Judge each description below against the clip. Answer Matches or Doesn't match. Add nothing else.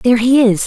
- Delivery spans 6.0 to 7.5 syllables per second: Matches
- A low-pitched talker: Doesn't match